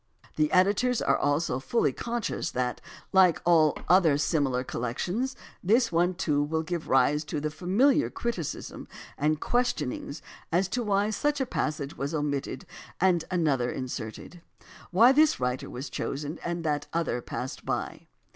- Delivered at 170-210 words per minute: No, average, 155 wpm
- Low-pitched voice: No, medium, 165 Hz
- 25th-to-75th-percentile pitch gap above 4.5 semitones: Yes, wide, 5.5 semitones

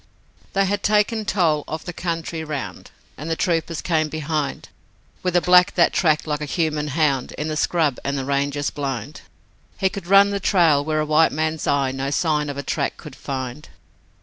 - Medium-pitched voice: Yes, medium, 155 Hz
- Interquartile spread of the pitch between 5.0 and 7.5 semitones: No, average, 3.2 semitones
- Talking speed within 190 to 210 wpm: Yes, average, 195 wpm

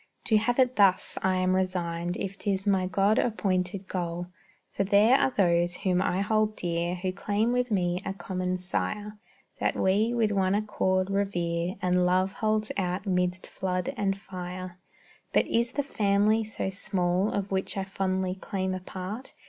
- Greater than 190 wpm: No, average, 170 wpm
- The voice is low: No, high, 190 Hz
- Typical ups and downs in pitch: No, narrow, 2.2 semitones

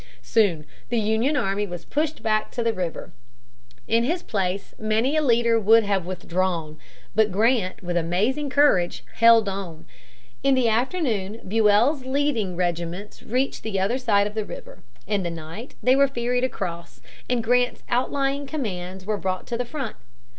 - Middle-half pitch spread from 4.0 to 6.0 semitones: Yes, average, 5.0 semitones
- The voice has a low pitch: No, high, 220 Hz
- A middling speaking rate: Yes, average, 160 wpm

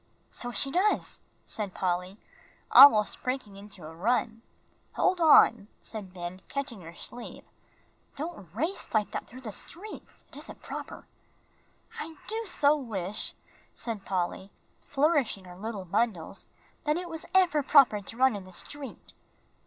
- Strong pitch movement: Yes, wide, 7.0 semitones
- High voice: Yes, high, 230 Hz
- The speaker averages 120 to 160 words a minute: Yes, average, 145 wpm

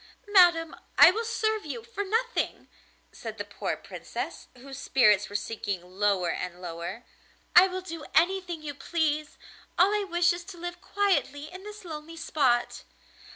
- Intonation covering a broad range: Yes, wide, 7.5 semitones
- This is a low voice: No, very high, 330 Hz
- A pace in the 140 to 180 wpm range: Yes, average, 155 wpm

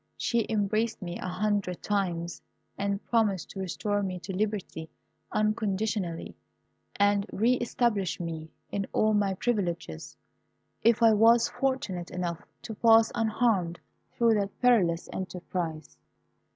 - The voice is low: No, high, 200 Hz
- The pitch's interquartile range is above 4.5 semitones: No, average, 3.6 semitones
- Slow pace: Yes, slow, 125 wpm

